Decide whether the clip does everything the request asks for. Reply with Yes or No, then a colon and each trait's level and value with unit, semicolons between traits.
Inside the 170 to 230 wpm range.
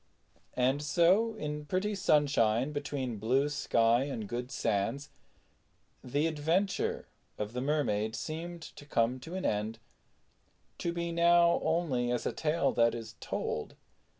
No: slow, 135 wpm